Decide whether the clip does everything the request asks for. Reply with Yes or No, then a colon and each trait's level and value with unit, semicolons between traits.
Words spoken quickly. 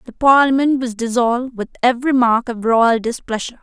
No: average, 165 wpm